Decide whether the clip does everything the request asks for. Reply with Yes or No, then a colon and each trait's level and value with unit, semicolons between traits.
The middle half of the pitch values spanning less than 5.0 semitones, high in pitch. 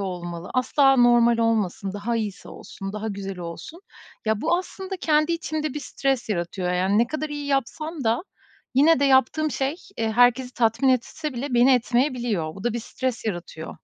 No: wide, 5.5 semitones; high, 240 Hz